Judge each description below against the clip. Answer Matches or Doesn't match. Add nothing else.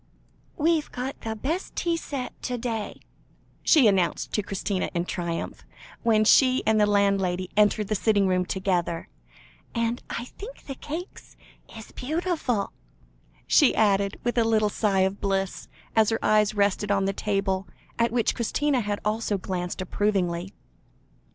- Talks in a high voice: Matches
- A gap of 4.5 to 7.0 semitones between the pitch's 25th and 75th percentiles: Doesn't match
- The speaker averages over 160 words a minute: Doesn't match